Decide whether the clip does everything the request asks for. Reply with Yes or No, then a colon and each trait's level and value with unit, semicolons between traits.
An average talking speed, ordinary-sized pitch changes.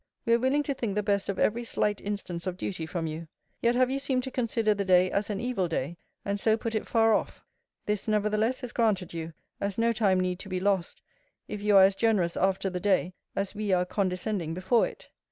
No: fast, 230 wpm; average, 3.5 semitones